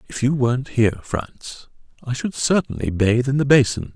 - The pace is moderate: Yes, average, 180 wpm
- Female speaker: No, male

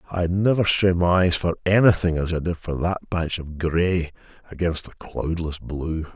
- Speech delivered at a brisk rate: No, average, 185 wpm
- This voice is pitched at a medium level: No, very low, 85 Hz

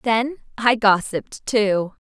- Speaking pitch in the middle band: No, high, 220 Hz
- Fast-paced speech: No, slow, 115 wpm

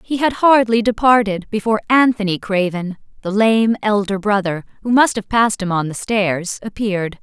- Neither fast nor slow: Yes, average, 165 wpm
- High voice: Yes, high, 210 Hz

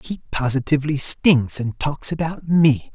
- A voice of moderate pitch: Yes, medium, 145 Hz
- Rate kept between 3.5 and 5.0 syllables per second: Yes, 4.4 syllables/s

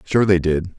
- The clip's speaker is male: Yes, male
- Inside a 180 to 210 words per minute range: No, fast, 230 wpm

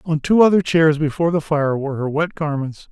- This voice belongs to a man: Yes, male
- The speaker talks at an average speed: No, fast, 225 wpm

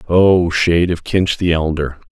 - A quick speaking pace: No, average, 170 wpm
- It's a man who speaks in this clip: Yes, male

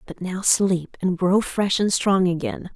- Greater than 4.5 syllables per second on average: No, 4.0 syllables/s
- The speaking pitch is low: No, medium, 185 Hz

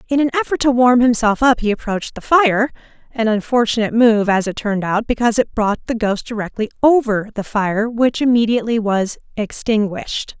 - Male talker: No, female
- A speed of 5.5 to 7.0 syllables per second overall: Yes, 5.6 syllables/s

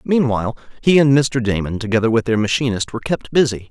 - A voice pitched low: Yes, low, 120 Hz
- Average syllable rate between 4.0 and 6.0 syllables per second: No, 6.3 syllables/s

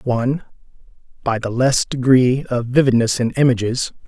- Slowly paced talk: Yes, slow, 130 wpm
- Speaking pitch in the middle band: No, low, 125 Hz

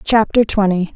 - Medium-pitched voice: No, high, 205 Hz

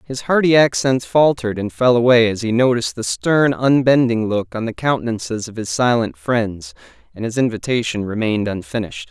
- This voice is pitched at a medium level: No, low, 115 Hz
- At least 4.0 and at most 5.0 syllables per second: No, 5.5 syllables/s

